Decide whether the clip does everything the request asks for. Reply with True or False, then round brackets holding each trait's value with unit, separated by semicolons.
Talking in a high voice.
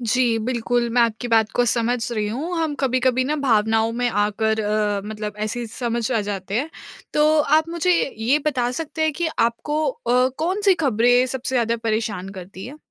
True (240 Hz)